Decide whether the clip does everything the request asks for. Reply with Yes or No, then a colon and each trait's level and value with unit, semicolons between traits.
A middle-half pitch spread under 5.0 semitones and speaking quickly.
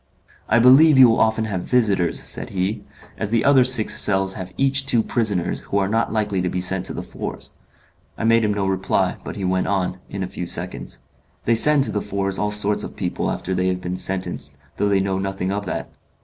Yes: average, 3.3 semitones; fast, 225 wpm